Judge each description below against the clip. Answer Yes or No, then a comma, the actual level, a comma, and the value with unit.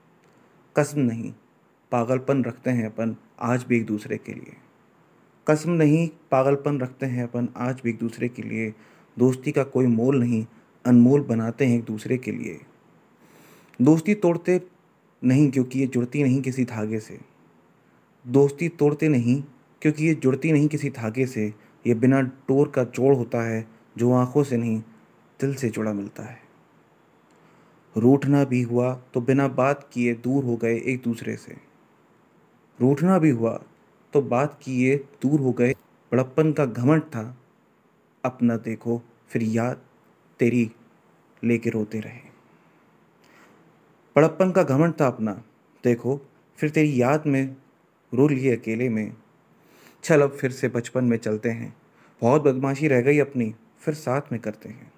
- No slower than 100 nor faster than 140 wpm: No, average, 150 wpm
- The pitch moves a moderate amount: Yes, average, 3.2 semitones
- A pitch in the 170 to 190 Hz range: No, low, 125 Hz